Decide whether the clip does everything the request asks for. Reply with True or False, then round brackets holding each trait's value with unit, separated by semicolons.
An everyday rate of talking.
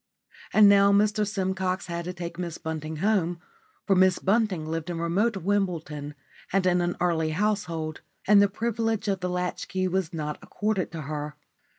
True (175 wpm)